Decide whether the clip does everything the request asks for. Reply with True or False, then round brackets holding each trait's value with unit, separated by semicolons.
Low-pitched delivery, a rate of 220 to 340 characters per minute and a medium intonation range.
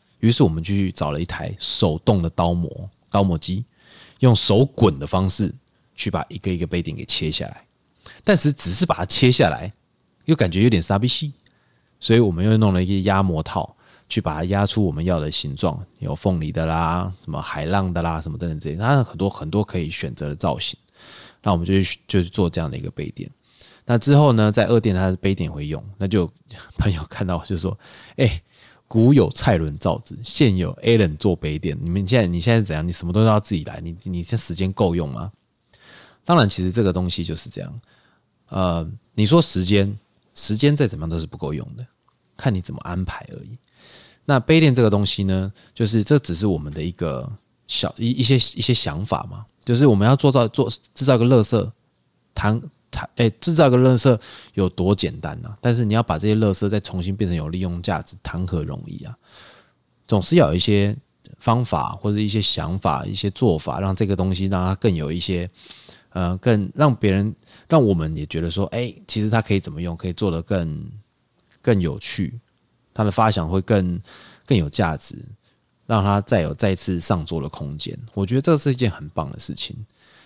True (100 Hz; 295 characters per minute; 4.9 semitones)